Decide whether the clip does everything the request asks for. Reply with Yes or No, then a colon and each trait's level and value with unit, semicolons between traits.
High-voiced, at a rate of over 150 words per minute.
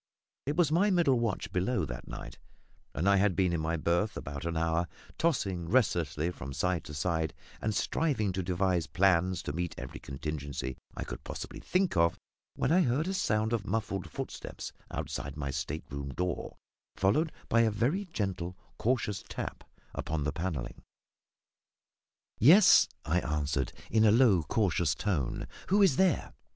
No: very low, 90 Hz; average, 165 wpm